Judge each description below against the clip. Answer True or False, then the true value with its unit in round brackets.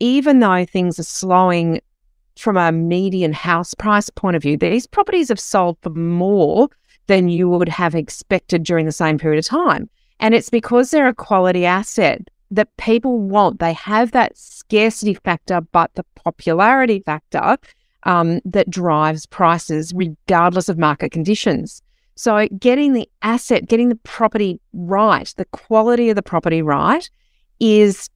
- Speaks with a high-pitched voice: True (195 Hz)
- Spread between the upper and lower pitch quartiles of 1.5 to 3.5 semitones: False (5.1 semitones)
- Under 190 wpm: True (155 wpm)